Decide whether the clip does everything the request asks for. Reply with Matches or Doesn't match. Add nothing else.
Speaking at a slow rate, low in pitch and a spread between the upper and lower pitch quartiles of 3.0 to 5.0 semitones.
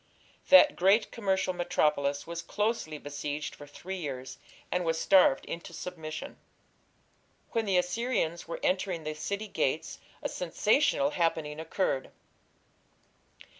Doesn't match